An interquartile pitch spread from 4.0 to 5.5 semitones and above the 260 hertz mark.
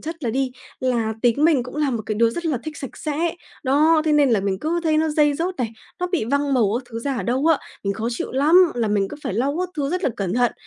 Yes: average, 5.0 semitones; very high, 275 Hz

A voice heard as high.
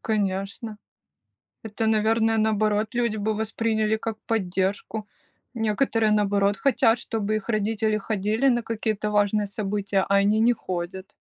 Yes: high, 215 Hz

